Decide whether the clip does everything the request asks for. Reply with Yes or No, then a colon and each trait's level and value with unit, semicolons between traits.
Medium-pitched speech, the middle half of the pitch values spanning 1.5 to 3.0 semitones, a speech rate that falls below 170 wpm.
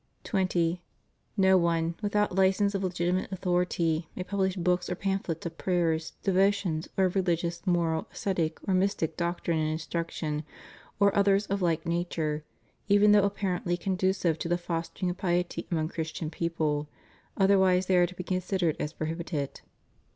Yes: medium, 175 Hz; narrow, 2.5 semitones; average, 160 wpm